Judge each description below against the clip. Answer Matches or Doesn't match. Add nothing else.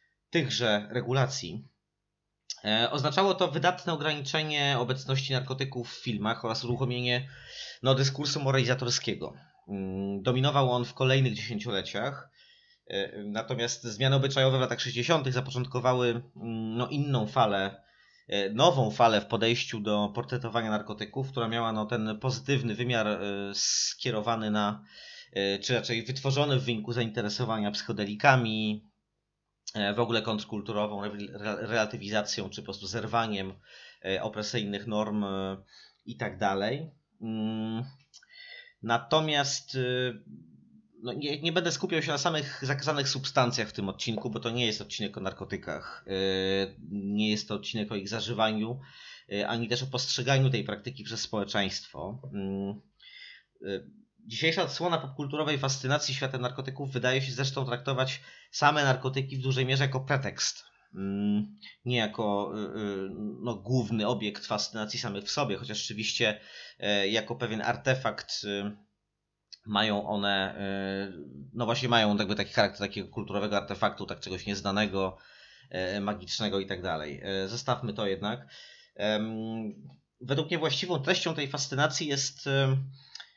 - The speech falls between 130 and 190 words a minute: Doesn't match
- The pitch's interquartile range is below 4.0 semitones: Doesn't match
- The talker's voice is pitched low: Matches